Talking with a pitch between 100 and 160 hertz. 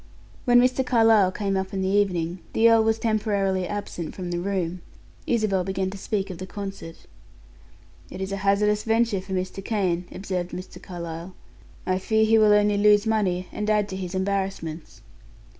No: high, 195 Hz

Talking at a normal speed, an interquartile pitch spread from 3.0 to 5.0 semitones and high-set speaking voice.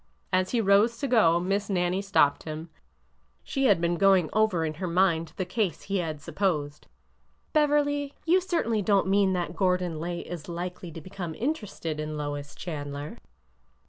No: average, 170 wpm; average, 4.0 semitones; medium, 180 Hz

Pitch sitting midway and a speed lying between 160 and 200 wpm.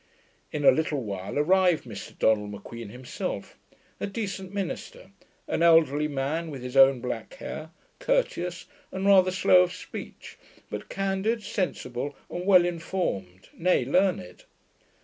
No: medium, 165 Hz; slow, 135 wpm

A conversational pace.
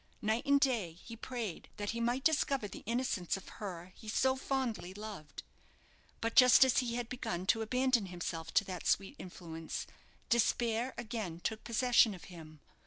Yes: average, 170 wpm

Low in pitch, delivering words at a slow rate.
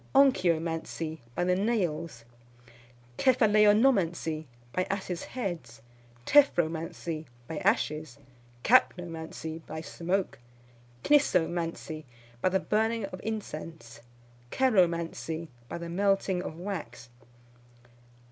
No: medium, 175 Hz; slow, 85 wpm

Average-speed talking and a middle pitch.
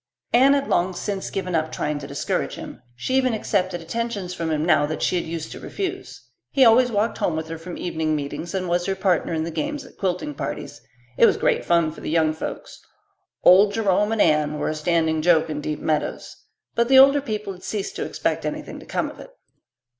No: fast, 220 wpm; medium, 175 Hz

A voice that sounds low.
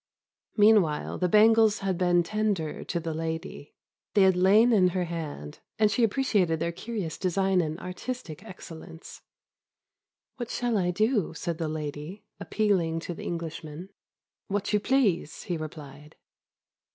No: medium, 180 Hz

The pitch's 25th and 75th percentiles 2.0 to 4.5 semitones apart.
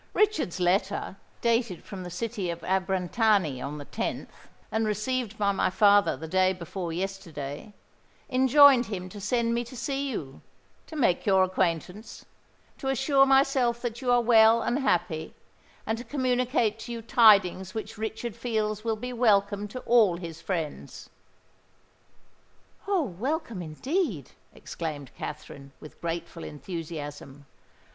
No: wide, 5.4 semitones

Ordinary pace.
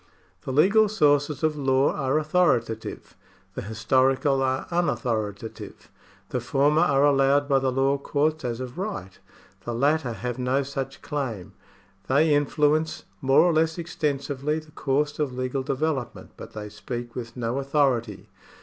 Yes: average, 145 wpm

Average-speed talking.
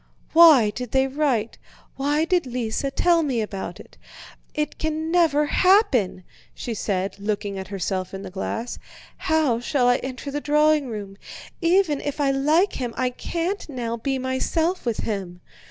Yes: average, 160 wpm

